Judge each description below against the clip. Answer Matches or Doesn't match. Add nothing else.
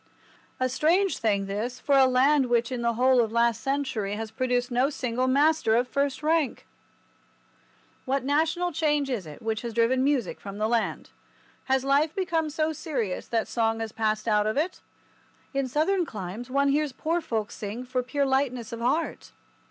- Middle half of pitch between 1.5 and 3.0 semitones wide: Doesn't match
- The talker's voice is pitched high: Matches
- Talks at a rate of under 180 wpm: Doesn't match